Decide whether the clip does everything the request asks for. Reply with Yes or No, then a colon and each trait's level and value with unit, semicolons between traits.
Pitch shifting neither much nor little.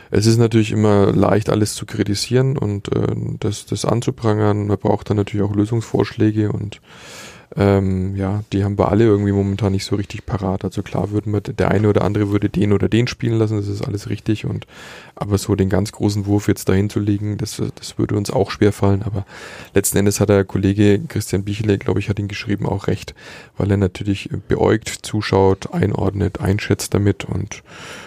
No: narrow, 1.4 semitones